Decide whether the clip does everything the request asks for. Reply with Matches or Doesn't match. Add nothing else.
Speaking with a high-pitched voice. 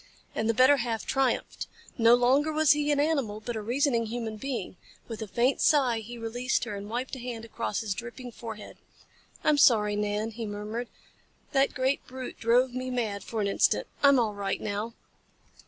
Matches